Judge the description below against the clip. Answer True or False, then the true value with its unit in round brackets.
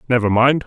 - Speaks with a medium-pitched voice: False (125 Hz)